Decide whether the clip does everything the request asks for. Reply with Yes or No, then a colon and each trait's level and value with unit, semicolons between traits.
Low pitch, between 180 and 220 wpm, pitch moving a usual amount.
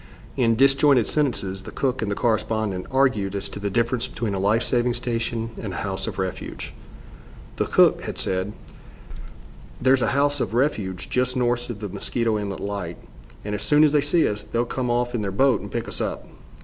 Yes: low, 115 Hz; average, 200 wpm; average, 4.0 semitones